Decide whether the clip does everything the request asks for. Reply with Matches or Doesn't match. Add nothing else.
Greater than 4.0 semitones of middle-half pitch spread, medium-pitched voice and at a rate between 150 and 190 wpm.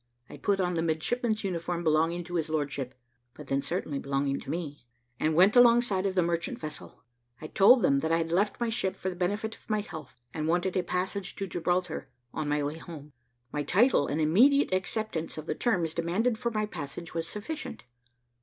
Doesn't match